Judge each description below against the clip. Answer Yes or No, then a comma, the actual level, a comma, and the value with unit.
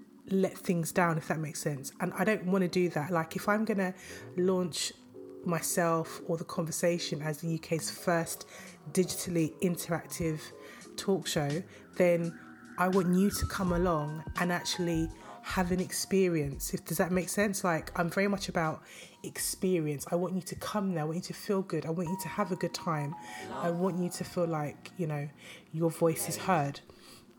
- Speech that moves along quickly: No, average, 190 wpm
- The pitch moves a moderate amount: No, narrow, 2.3 semitones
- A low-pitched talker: No, medium, 175 Hz